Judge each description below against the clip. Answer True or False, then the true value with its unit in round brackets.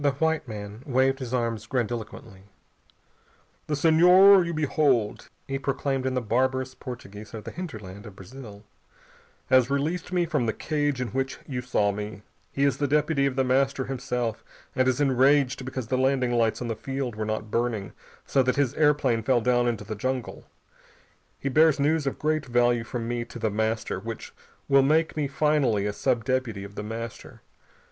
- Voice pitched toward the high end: False (130 Hz)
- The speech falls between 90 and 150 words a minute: False (185 wpm)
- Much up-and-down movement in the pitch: False (3.5 semitones)